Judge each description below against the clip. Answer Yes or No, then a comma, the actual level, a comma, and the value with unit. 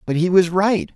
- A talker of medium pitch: Yes, medium, 175 Hz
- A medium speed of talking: No, fast, 250 wpm